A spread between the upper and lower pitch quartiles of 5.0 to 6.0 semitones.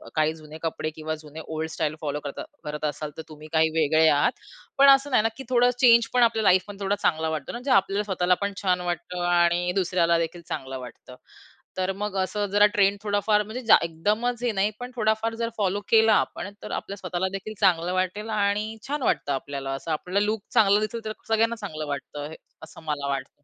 Yes: average, 5.3 semitones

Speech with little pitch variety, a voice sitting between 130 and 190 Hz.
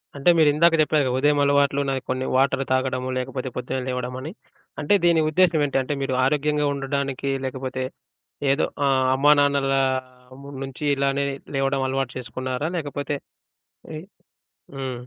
Yes: narrow, 1.9 semitones; low, 135 Hz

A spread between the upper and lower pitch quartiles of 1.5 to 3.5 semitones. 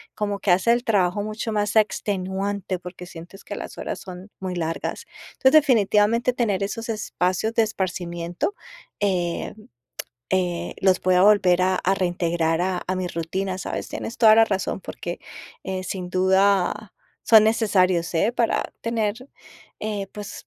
Yes: average, 2.9 semitones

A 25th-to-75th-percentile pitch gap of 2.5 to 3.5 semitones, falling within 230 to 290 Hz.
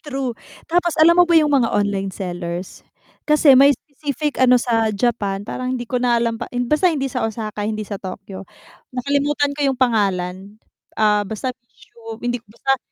No: wide, 5.4 semitones; high, 245 Hz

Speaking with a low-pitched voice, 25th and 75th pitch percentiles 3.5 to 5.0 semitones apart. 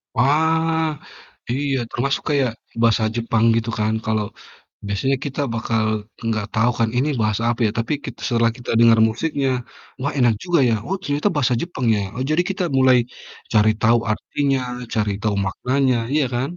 Yes: low, 125 Hz; average, 4.2 semitones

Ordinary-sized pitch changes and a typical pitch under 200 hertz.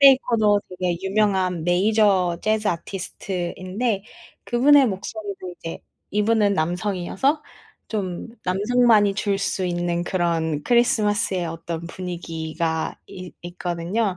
Yes: average, 3.5 semitones; high, 190 Hz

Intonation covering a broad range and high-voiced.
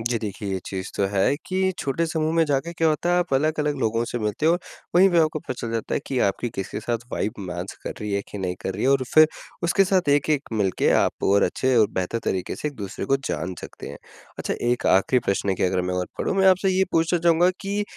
No: wide, 8.6 semitones; low, 130 Hz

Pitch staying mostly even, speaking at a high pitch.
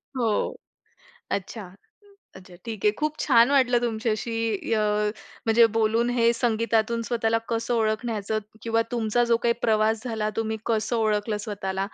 Yes: narrow, 1.4 semitones; high, 225 Hz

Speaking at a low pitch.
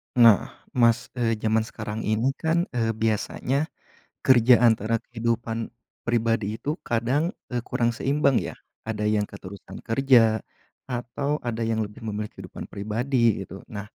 Yes: low, 115 Hz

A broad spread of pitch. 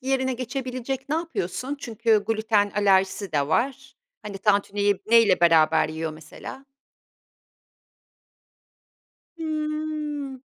Yes: wide, 5.7 semitones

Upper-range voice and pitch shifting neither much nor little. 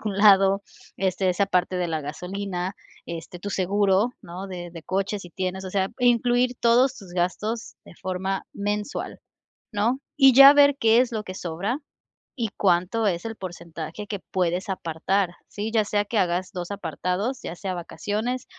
Yes: high, 195 Hz; average, 3.3 semitones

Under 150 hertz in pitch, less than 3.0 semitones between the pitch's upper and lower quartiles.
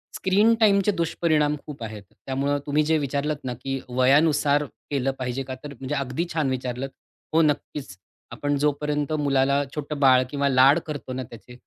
Yes: medium, 140 Hz; narrow, 2.4 semitones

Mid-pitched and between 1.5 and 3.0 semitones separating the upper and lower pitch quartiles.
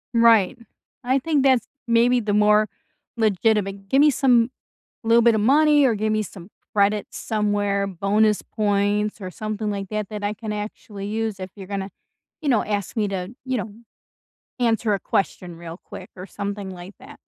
No: high, 210 Hz; narrow, 2.4 semitones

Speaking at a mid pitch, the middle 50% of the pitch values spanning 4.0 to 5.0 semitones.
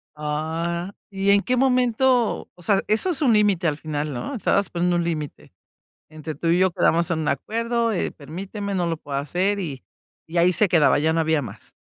Yes: medium, 175 Hz; average, 4.7 semitones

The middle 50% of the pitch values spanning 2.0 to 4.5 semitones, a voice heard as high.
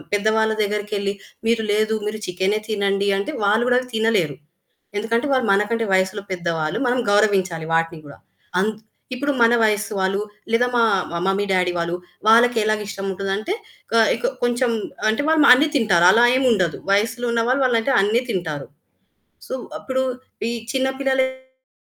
Yes: average, 3.7 semitones; high, 215 Hz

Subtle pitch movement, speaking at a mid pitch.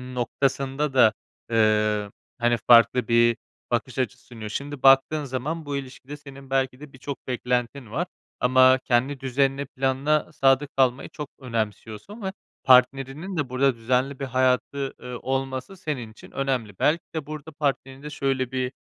No: narrow, 2.1 semitones; low, 130 Hz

